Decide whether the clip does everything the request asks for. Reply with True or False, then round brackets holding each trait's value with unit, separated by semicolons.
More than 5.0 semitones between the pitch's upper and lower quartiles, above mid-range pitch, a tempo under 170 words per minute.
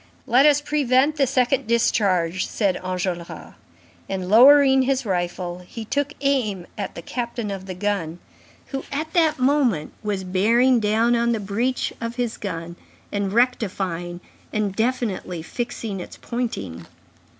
True (5.5 semitones; 220 Hz; 140 wpm)